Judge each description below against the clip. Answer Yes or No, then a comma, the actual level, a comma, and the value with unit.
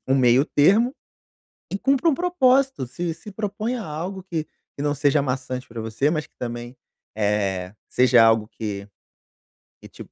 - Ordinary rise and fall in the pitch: No, wide, 8.9 semitones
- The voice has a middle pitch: Yes, medium, 145 Hz